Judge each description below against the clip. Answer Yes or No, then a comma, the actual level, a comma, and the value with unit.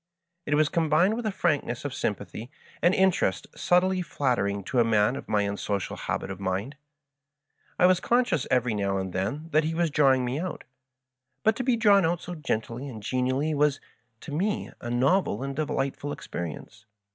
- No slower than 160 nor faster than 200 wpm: Yes, average, 180 wpm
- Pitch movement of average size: No, wide, 7.8 semitones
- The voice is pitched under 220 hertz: Yes, medium, 140 Hz